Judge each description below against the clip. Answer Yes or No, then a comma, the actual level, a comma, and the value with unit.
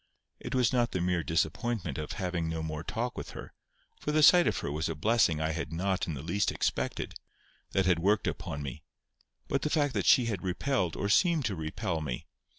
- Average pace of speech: No, fast, 215 wpm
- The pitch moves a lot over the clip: Yes, wide, 6.8 semitones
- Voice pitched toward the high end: No, very low, 90 Hz